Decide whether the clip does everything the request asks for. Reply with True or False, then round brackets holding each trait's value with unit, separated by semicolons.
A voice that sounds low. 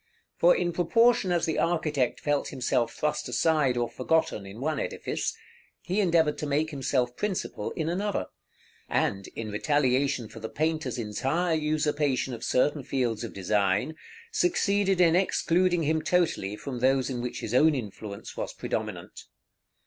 False (145 Hz)